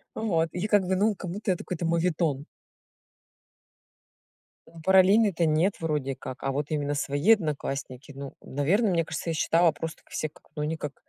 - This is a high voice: No, medium, 165 Hz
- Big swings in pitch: No, average, 4.2 semitones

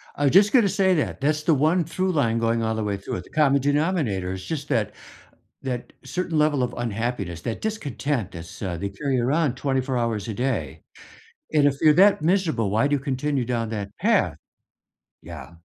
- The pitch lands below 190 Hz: Yes, low, 135 Hz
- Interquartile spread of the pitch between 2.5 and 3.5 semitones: No, wide, 5.5 semitones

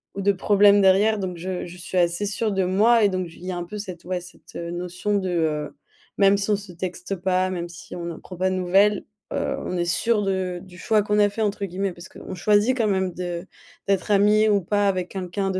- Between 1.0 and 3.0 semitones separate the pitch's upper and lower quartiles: Yes, narrow, 2.4 semitones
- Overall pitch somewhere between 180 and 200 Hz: Yes, high, 190 Hz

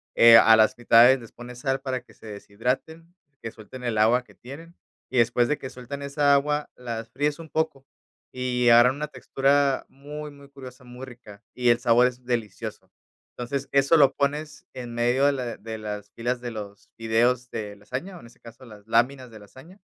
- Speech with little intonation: No, average, 3.2 semitones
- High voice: No, low, 125 Hz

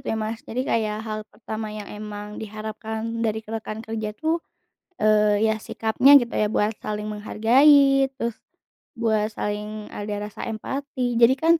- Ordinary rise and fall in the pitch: No, narrow, 1.7 semitones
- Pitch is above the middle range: Yes, high, 220 Hz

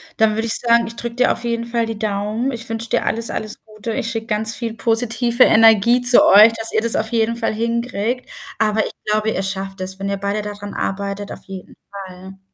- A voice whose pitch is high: Yes, high, 220 Hz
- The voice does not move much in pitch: Yes, narrow, 2.3 semitones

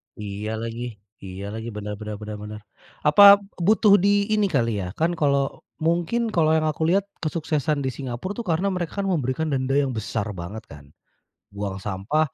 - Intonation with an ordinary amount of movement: No, wide, 8.2 semitones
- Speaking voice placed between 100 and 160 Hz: Yes, medium, 140 Hz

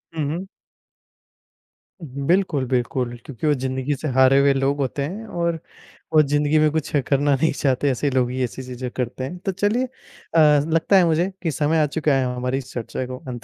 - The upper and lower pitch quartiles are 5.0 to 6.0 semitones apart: No, average, 3.5 semitones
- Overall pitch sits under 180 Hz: Yes, medium, 140 Hz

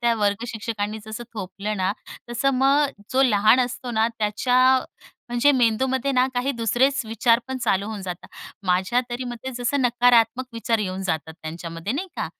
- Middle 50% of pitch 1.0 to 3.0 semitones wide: No, average, 3.7 semitones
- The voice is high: Yes, high, 230 Hz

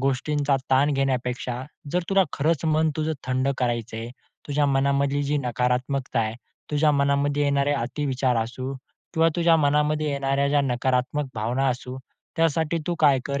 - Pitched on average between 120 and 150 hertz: Yes, medium, 140 Hz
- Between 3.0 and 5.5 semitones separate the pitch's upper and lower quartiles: No, narrow, 2.5 semitones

